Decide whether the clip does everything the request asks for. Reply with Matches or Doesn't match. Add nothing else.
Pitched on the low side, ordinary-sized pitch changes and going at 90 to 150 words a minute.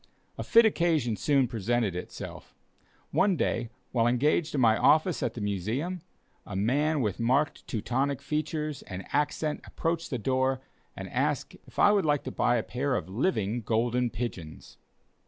Doesn't match